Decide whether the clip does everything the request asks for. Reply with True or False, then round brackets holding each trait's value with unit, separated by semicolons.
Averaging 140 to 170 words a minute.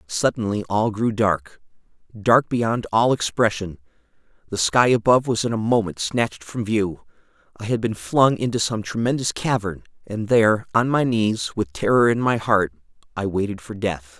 True (165 wpm)